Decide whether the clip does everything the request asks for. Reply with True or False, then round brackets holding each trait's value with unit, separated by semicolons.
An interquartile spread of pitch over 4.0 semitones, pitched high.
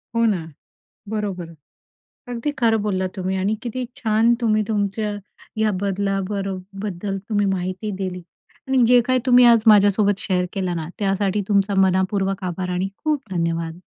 False (2.6 semitones; 200 Hz)